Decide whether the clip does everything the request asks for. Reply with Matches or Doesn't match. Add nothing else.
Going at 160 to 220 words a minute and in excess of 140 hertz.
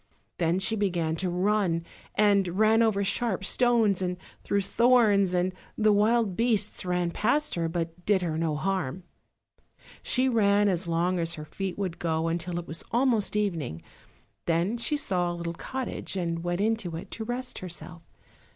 Matches